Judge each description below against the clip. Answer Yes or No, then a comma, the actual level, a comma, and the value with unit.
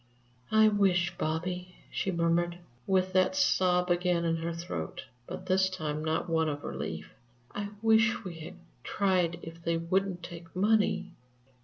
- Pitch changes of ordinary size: No, narrow, 2.2 semitones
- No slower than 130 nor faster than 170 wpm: Yes, average, 150 wpm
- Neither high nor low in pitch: Yes, medium, 180 Hz